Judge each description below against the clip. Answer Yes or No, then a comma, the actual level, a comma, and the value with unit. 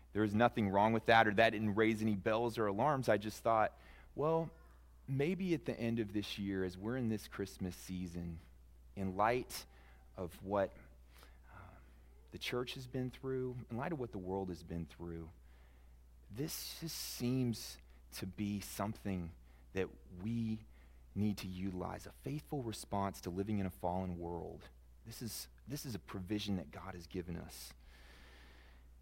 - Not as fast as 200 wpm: Yes, average, 170 wpm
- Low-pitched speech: Yes, very low, 95 Hz